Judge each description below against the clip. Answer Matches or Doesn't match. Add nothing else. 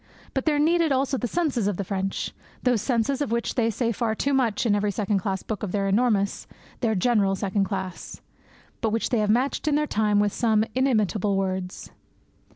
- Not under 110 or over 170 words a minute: Doesn't match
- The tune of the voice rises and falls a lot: Doesn't match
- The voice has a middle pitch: Doesn't match